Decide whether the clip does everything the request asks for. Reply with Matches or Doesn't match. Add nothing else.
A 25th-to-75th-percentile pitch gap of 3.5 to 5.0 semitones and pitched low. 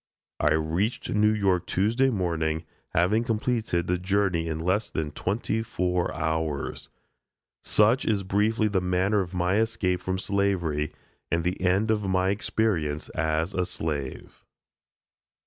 Matches